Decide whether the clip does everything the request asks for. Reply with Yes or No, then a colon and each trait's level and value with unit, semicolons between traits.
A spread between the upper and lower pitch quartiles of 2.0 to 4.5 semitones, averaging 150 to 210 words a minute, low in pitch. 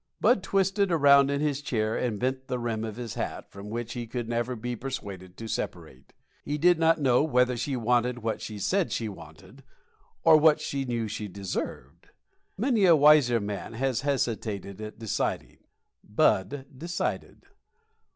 No: average, 4.9 semitones; average, 165 wpm; low, 125 Hz